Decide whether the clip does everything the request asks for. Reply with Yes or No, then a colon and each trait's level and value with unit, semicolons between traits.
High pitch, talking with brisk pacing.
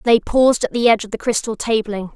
Yes: high, 225 Hz; fast, 250 wpm